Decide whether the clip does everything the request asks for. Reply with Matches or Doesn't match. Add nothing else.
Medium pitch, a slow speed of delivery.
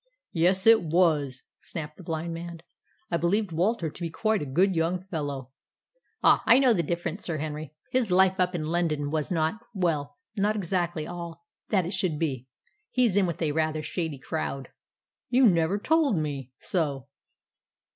Doesn't match